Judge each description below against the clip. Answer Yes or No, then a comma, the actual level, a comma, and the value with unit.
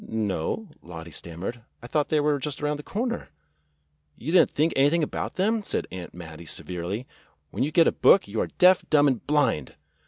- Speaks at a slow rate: No, average, 195 wpm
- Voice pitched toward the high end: No, medium, 140 Hz